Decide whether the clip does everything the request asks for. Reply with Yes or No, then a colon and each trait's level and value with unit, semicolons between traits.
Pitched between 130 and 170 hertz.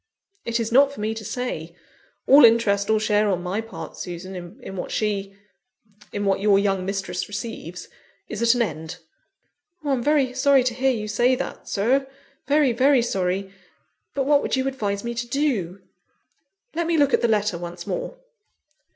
No: high, 225 Hz